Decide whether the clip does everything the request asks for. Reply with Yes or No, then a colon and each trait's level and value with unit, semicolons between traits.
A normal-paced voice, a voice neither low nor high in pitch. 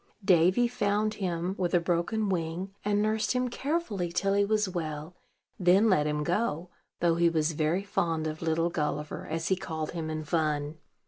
Yes: average, 180 wpm; medium, 175 Hz